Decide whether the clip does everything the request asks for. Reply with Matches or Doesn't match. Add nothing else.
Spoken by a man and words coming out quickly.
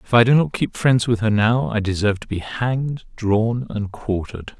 Matches